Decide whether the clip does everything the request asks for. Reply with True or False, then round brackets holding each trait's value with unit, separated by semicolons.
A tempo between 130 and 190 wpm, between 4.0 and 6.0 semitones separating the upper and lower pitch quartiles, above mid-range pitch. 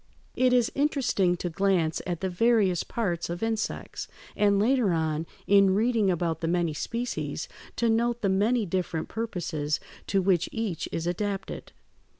True (155 wpm; 4.7 semitones; 195 Hz)